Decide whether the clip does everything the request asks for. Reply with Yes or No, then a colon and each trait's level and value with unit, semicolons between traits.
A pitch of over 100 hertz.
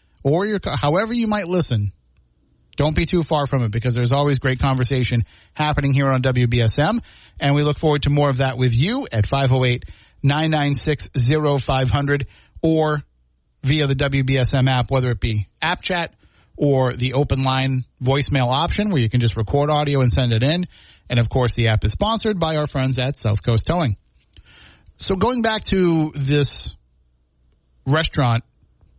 Yes: low, 135 Hz